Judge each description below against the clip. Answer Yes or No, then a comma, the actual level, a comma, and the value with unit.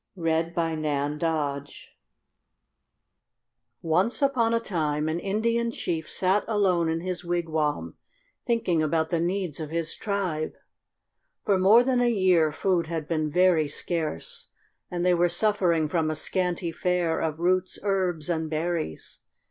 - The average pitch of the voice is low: No, medium, 170 Hz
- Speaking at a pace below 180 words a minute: Yes, average, 140 wpm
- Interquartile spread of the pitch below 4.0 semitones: Yes, average, 2.9 semitones